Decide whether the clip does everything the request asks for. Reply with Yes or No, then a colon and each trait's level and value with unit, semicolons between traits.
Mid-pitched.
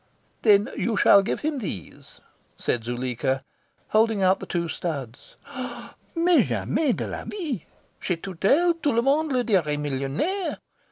No: high, 200 Hz